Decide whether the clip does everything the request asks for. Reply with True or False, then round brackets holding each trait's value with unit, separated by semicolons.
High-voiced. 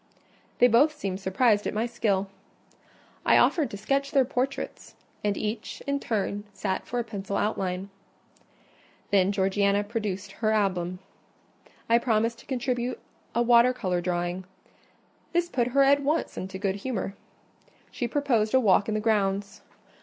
True (215 Hz)